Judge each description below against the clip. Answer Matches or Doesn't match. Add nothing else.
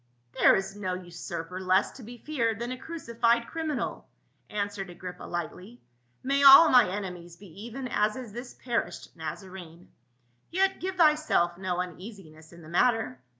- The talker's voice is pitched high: Matches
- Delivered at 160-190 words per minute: Matches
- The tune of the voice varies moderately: Doesn't match